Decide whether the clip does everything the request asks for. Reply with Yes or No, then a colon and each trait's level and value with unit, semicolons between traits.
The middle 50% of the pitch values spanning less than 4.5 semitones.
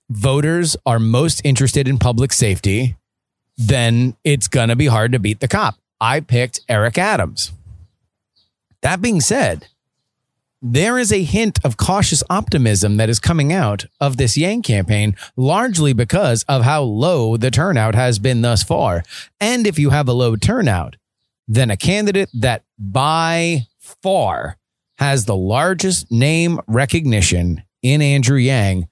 No: average, 4.9 semitones